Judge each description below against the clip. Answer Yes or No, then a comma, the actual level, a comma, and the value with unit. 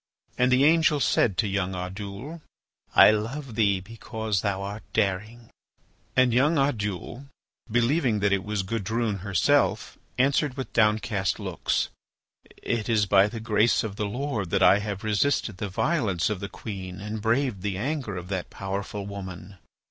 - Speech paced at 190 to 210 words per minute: No, average, 155 wpm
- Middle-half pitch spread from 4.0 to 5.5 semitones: No, average, 3.4 semitones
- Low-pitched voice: Yes, low, 105 Hz